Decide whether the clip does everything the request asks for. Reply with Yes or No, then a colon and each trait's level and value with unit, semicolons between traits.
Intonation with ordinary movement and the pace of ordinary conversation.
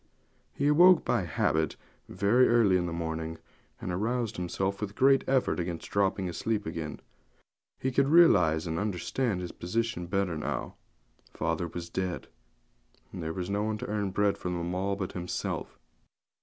Yes: average, 4.1 semitones; average, 165 wpm